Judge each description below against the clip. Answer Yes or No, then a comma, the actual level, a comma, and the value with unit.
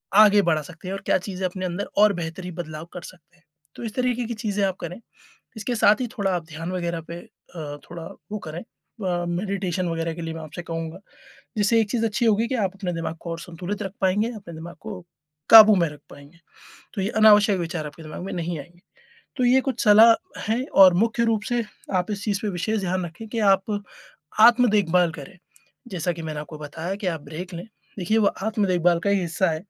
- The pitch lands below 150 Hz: No, medium, 185 Hz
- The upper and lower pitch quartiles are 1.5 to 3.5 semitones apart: No, average, 4.0 semitones